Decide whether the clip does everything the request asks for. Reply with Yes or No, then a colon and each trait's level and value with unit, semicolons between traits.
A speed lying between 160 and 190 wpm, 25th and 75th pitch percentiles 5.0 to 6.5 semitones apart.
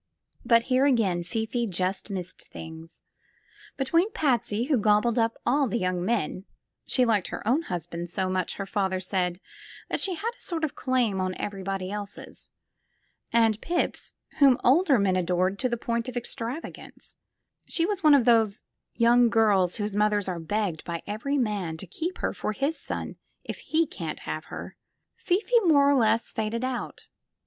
Yes: average, 170 wpm; wide, 5.4 semitones